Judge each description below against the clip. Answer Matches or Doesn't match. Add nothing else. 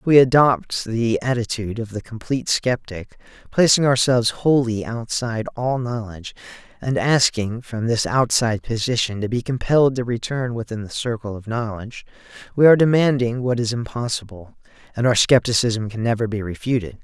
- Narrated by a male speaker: Matches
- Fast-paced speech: Doesn't match